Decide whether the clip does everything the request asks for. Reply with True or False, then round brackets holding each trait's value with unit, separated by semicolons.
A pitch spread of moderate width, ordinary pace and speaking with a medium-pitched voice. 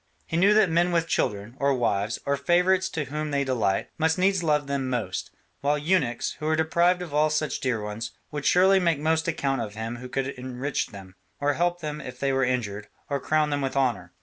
False (4.5 semitones; 220 wpm; 145 Hz)